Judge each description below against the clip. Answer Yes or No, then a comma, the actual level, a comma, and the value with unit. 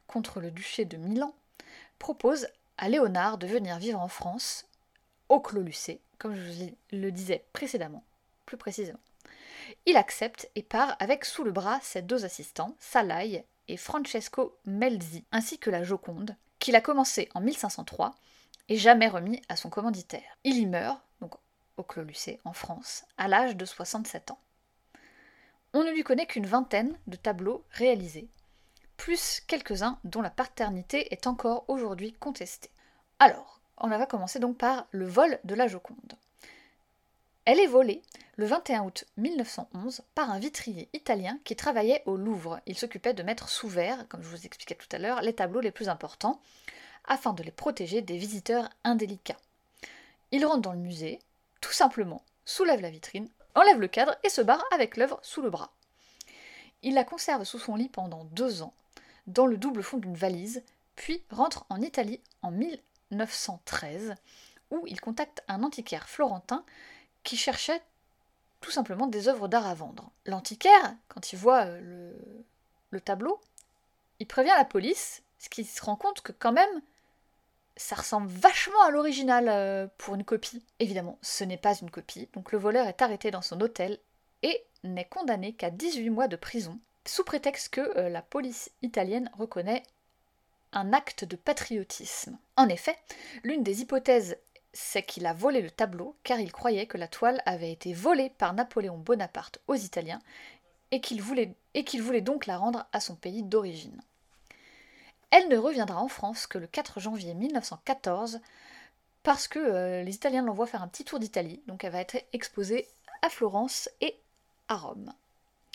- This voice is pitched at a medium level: No, high, 230 Hz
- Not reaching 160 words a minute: No, average, 165 wpm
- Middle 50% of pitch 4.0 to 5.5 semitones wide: Yes, average, 5.1 semitones